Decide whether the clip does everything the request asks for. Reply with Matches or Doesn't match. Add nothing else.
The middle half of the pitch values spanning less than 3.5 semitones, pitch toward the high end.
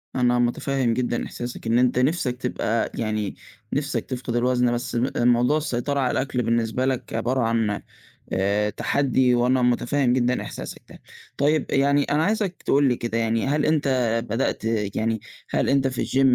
Doesn't match